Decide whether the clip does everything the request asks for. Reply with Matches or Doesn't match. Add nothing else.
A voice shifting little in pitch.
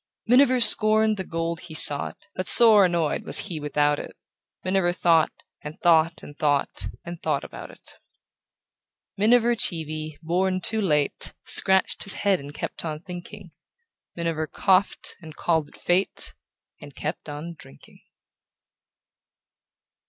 Doesn't match